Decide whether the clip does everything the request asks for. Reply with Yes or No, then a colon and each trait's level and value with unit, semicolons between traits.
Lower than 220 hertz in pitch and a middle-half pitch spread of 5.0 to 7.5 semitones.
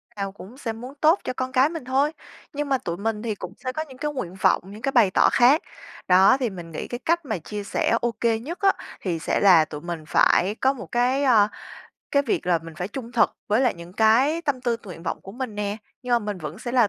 No: high, 230 Hz; average, 5.3 semitones